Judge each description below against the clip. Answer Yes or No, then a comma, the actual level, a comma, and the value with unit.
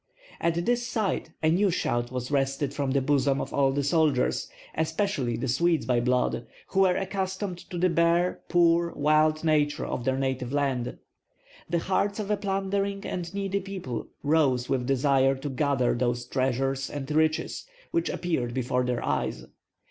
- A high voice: No, medium, 145 Hz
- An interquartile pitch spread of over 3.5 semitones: Yes, average, 5.1 semitones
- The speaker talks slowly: No, average, 165 wpm